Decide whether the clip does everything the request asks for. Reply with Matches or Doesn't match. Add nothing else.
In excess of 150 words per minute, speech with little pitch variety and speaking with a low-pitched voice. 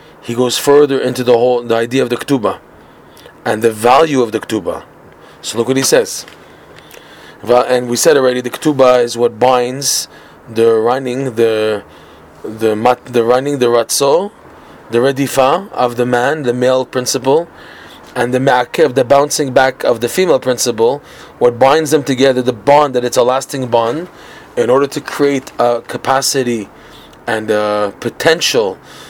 Matches